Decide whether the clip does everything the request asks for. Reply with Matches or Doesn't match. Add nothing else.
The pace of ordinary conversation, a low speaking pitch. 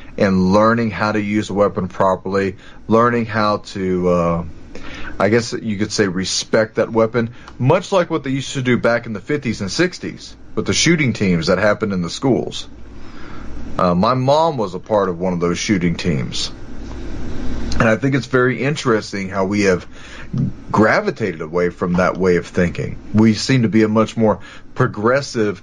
Matches